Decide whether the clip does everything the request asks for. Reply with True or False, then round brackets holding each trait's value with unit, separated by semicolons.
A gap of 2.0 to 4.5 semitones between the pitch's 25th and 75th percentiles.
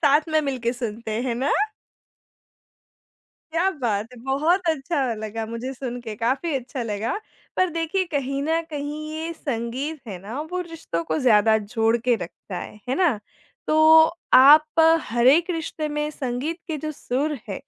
False (5.1 semitones)